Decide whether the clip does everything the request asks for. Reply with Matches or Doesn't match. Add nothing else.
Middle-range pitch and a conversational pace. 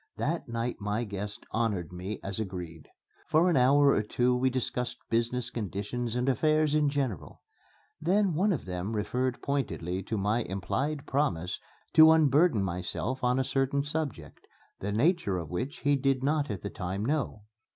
Doesn't match